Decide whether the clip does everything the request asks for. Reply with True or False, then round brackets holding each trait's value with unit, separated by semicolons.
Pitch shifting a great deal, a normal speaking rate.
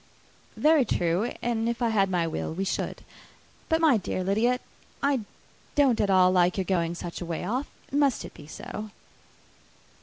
True (5.7 semitones; 175 wpm)